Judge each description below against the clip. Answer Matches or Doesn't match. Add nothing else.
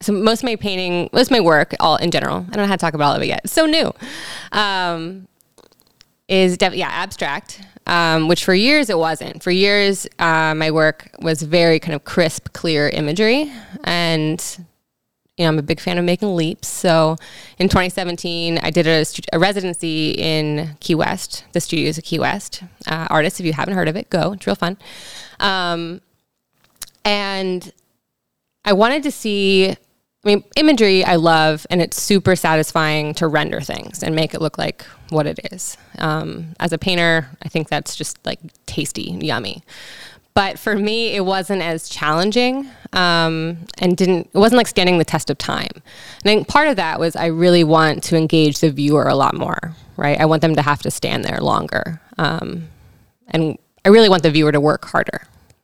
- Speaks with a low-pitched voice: Doesn't match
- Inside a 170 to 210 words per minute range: Matches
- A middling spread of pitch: Matches